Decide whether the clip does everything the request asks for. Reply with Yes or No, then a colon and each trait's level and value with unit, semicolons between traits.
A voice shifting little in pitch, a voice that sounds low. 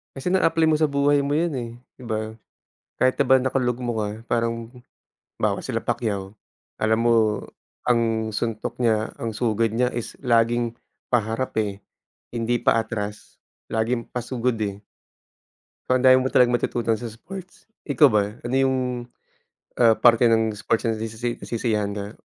Yes: narrow, 2.3 semitones; low, 115 Hz